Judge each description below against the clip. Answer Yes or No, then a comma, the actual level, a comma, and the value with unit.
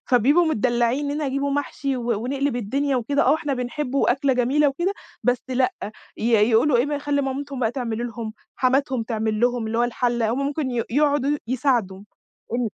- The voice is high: Yes, very high, 255 Hz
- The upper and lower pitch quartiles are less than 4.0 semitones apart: Yes, average, 2.9 semitones